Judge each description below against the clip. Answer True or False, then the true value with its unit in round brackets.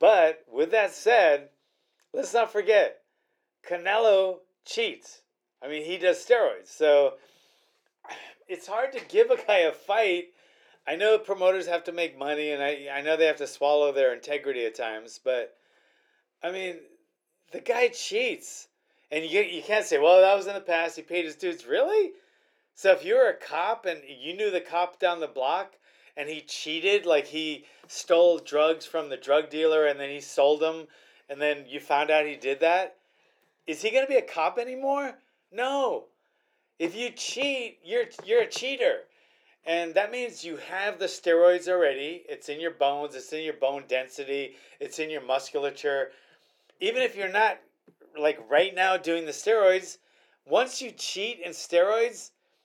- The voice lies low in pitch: False (185 Hz)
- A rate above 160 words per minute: True (175 wpm)